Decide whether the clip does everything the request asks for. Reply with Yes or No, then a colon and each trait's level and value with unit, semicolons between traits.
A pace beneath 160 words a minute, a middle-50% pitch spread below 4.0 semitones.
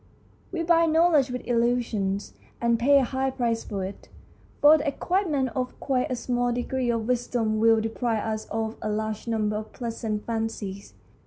No: average, 170 wpm; average, 3.1 semitones